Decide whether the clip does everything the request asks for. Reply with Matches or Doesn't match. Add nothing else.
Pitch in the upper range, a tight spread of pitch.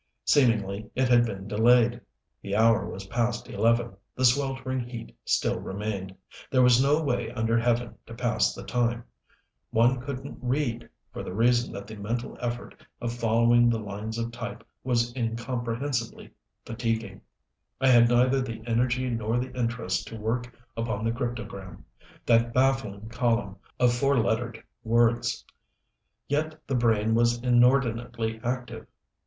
Doesn't match